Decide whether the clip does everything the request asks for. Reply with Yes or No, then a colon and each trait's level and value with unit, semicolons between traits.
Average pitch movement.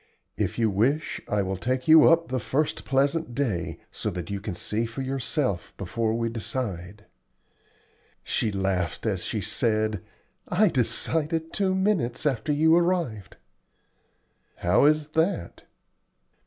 No: wide, 7.0 semitones